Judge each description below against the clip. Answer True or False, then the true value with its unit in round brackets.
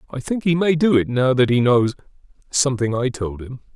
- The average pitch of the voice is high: False (130 Hz)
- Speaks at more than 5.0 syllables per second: True (5.5 syllables/s)